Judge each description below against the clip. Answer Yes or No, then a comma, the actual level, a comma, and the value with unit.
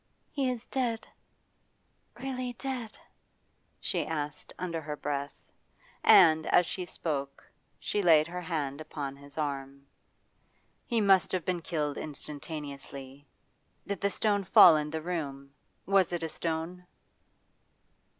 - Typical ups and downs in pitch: Yes, average, 4.5 semitones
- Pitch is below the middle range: No, medium, 160 Hz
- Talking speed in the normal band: No, slow, 125 wpm